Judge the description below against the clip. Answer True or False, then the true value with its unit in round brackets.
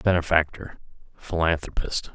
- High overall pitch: False (80 Hz)